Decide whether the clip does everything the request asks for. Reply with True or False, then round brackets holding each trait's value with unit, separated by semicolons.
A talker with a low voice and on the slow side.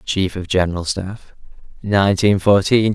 True (100 Hz; 120 wpm)